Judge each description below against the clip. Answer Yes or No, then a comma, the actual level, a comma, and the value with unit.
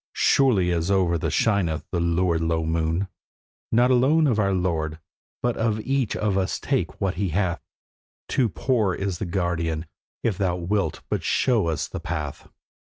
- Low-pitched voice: Yes, very low, 95 Hz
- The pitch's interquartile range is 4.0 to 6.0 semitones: Yes, average, 4.3 semitones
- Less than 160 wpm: No, average, 170 wpm